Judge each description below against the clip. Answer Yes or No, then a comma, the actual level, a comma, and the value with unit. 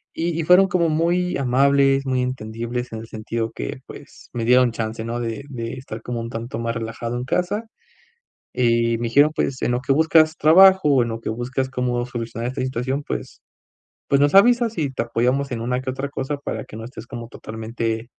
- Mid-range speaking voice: No, low, 125 Hz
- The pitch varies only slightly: No, average, 3.4 semitones